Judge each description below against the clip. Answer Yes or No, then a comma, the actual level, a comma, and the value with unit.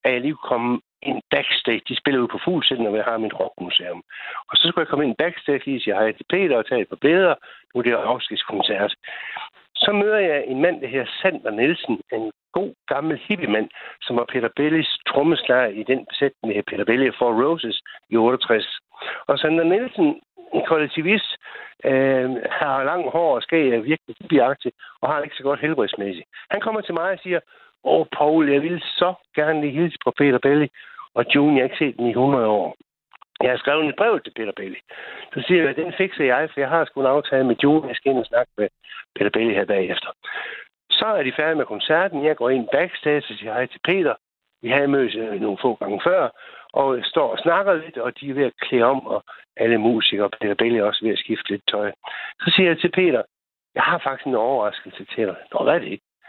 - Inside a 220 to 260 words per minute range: Yes, fast, 225 wpm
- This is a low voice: No, medium, 145 Hz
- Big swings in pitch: Yes, wide, 6.1 semitones